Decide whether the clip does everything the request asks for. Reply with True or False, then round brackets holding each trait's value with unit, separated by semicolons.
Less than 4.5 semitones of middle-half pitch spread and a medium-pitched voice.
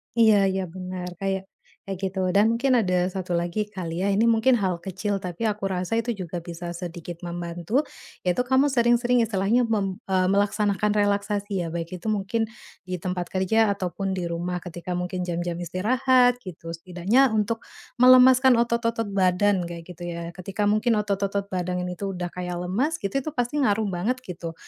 False (3.9 semitones; 195 Hz)